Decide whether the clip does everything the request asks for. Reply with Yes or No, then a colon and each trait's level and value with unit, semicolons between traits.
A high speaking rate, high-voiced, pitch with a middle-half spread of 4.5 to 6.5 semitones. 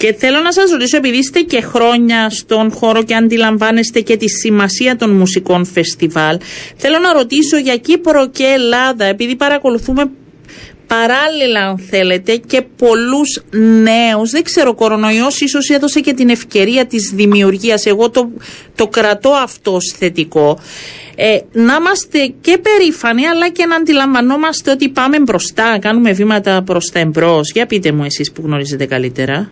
No: average, 155 wpm; high, 230 Hz; average, 5.3 semitones